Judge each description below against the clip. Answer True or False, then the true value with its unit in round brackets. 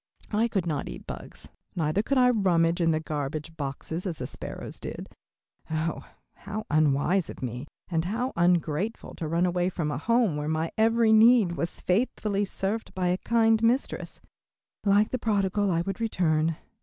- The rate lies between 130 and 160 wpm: False (170 wpm)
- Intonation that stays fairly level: False (5.4 semitones)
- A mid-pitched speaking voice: True (180 Hz)